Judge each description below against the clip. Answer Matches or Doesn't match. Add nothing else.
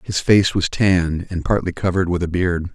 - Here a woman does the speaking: Doesn't match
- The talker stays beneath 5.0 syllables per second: Doesn't match